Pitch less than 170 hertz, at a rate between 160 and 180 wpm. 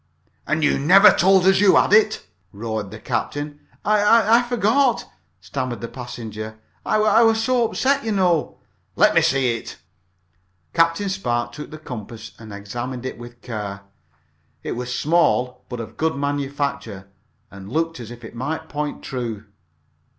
Yes: medium, 140 Hz; average, 165 wpm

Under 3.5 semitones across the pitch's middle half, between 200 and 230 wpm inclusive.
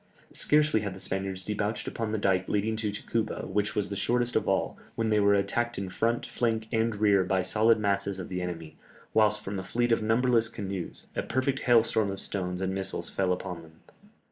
Yes: average, 2.8 semitones; fast, 205 wpm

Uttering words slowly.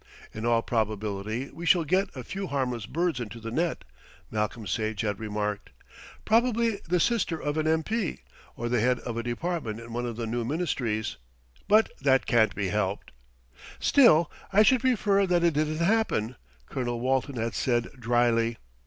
No: average, 170 wpm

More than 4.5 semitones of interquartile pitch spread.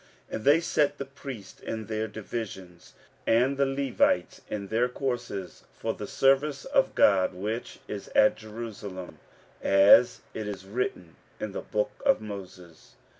Yes: wide, 5.4 semitones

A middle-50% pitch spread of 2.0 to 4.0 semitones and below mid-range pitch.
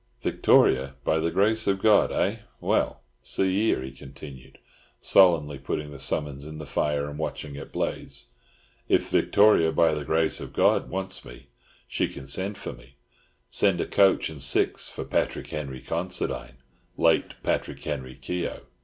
No: average, 4.6 semitones; very low, 75 Hz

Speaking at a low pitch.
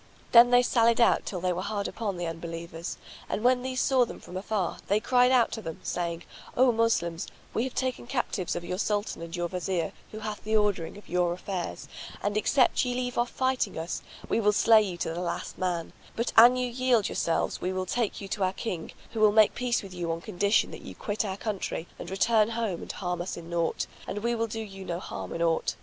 No: high, 205 Hz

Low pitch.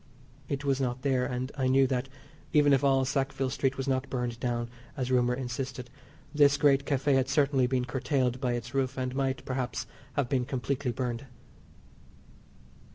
Yes: low, 130 Hz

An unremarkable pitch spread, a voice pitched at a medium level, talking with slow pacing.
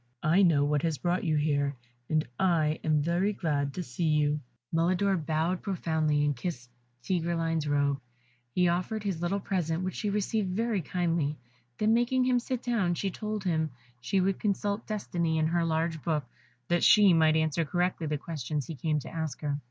No: average, 3.6 semitones; medium, 165 Hz; average, 185 wpm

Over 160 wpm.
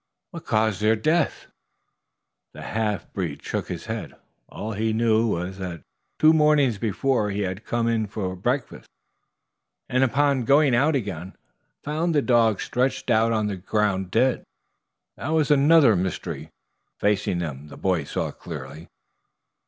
No: average, 150 wpm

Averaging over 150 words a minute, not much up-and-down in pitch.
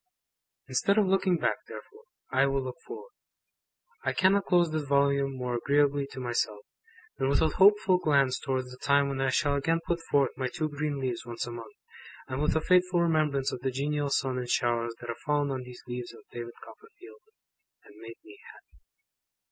No: average, 195 wpm; average, 4.5 semitones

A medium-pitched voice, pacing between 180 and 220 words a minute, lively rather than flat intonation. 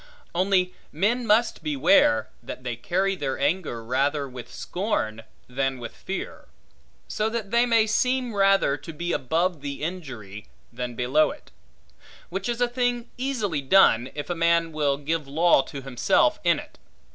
No: medium, 170 Hz; average, 155 wpm; wide, 7.8 semitones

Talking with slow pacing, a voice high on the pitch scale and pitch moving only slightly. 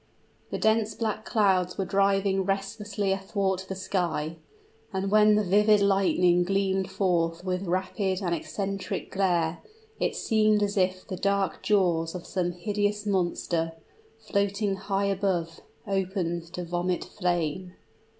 Yes: slow, 130 wpm; high, 195 Hz; narrow, 2.0 semitones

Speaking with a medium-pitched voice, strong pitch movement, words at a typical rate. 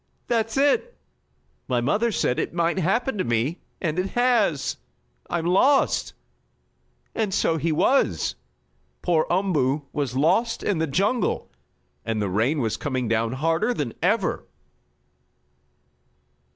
No: medium, 170 Hz; wide, 8.3 semitones; slow, 125 wpm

